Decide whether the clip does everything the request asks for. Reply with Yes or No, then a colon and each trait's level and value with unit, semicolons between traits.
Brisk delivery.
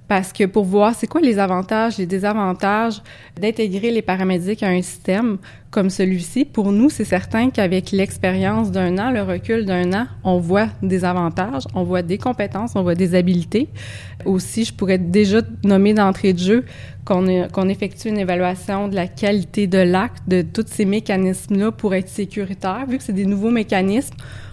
No: average, 185 wpm